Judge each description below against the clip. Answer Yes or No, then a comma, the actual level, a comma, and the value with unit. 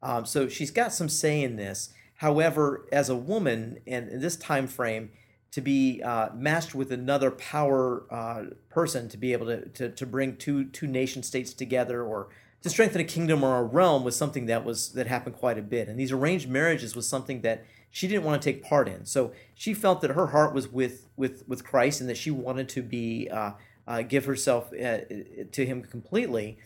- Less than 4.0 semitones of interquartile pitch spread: Yes, average, 3.3 semitones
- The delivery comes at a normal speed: No, fast, 210 wpm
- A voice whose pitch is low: Yes, low, 130 Hz